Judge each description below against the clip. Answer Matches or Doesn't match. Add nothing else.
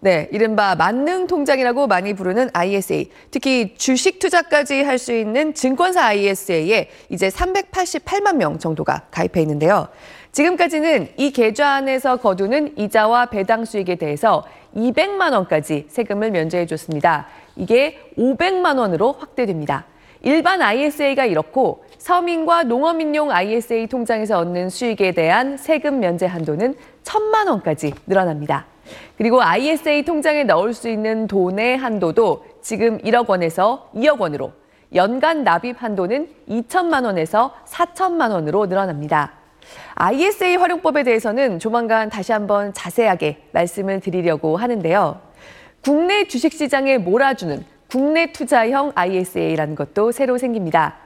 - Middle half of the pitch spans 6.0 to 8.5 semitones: Matches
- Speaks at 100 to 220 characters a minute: Doesn't match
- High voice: Matches